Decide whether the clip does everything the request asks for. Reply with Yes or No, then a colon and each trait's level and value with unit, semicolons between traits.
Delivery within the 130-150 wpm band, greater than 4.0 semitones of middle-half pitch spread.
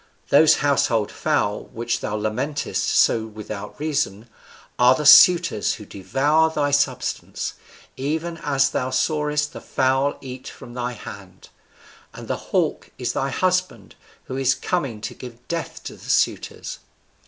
Yes: average, 140 wpm; average, 4.5 semitones